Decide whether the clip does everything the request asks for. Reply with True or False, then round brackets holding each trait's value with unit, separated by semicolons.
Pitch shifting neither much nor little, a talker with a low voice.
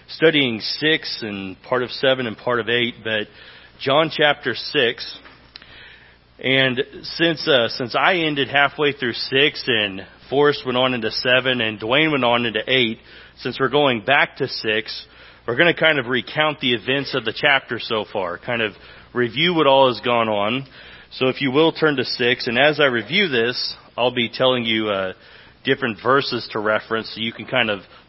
True (3.9 semitones; 125 Hz)